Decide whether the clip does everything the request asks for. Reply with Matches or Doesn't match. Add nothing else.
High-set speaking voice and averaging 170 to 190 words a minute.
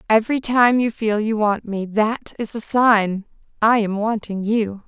Matches